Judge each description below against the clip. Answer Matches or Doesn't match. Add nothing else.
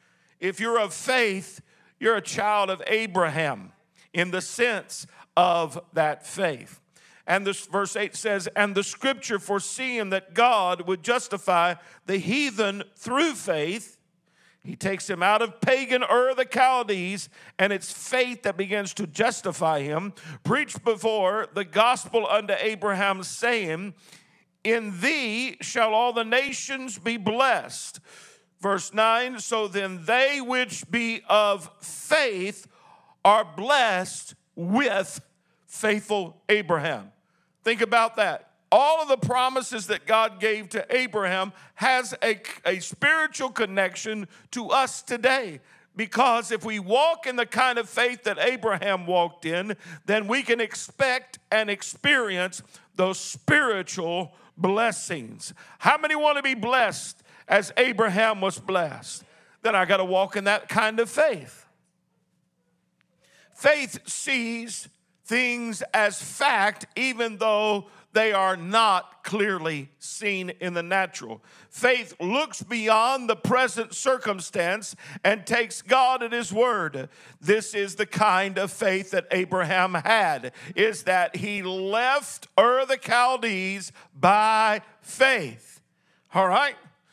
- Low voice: Doesn't match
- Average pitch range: Matches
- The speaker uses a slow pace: Matches